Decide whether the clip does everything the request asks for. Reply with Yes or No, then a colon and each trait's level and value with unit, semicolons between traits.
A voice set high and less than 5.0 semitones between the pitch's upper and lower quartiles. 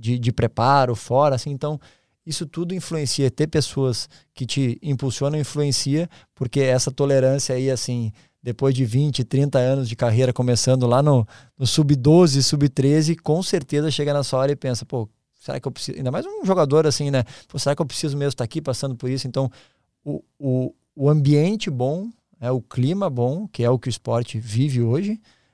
No: low, 135 Hz; average, 2.9 semitones